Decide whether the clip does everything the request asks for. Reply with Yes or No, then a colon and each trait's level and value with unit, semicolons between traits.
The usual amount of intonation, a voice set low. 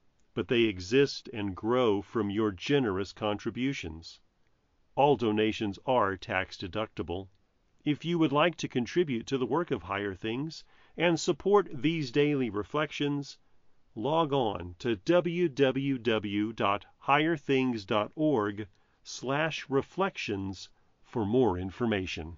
No: wide, 5.9 semitones; low, 120 Hz